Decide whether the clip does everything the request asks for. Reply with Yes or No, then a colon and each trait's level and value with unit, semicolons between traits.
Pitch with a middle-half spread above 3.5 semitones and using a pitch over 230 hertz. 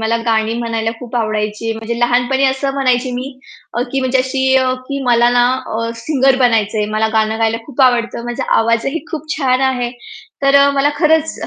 No: average, 3.0 semitones; high, 245 Hz